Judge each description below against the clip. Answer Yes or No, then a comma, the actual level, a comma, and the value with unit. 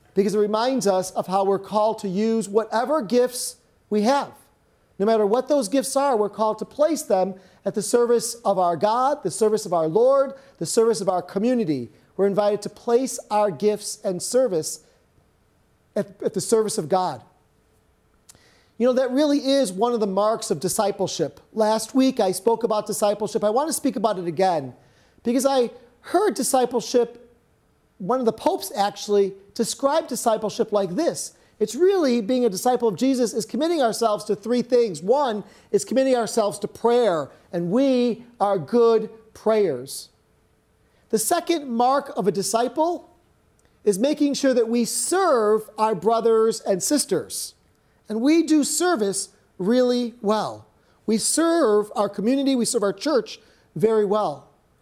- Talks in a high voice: Yes, high, 225 Hz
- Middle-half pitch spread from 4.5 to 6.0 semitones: No, average, 3.6 semitones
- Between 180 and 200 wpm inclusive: No, average, 160 wpm